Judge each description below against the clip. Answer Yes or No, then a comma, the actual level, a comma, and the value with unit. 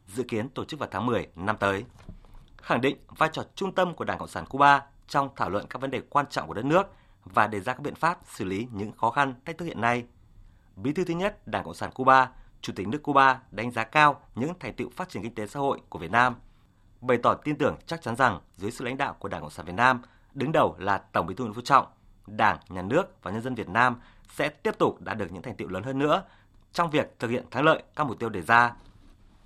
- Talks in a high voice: No, low, 120 Hz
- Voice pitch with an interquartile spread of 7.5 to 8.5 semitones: No, average, 5.2 semitones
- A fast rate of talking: Yes, fast, 265 wpm